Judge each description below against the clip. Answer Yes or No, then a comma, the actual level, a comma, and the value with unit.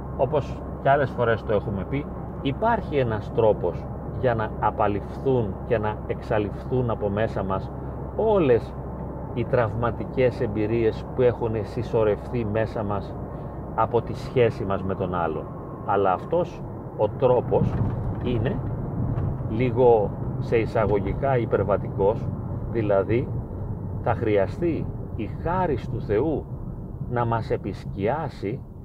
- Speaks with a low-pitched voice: Yes, low, 115 Hz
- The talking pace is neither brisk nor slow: No, slow, 110 wpm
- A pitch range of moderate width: Yes, average, 3.0 semitones